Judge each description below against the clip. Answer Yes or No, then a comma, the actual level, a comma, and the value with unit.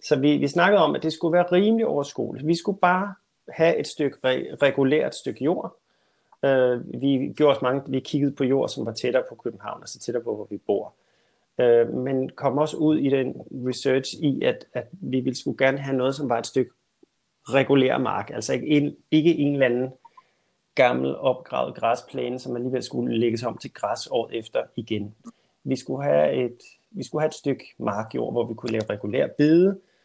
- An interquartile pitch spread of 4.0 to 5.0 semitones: No, average, 3.2 semitones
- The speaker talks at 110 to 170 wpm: No, average, 200 wpm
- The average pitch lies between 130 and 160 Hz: Yes, low, 135 Hz